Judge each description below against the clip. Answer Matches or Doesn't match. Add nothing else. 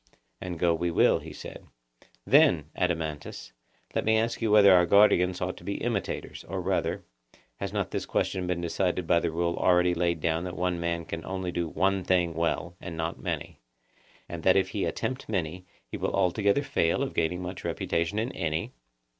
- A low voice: Matches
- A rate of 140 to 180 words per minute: Doesn't match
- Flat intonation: Matches